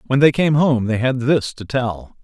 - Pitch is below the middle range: Yes, low, 125 Hz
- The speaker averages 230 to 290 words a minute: Yes, fast, 240 wpm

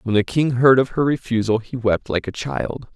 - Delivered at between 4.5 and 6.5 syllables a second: Yes, 5.0 syllables/s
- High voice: No, low, 120 Hz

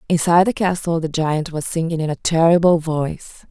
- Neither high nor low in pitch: Yes, medium, 165 Hz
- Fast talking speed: No, average, 190 wpm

